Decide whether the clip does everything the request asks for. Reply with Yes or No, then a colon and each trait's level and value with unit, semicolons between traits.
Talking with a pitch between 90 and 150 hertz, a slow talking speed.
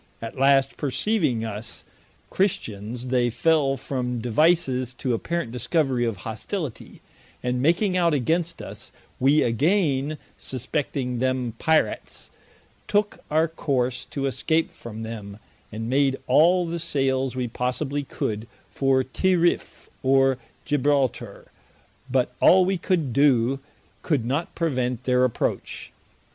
Yes: low, 135 Hz; slow, 120 wpm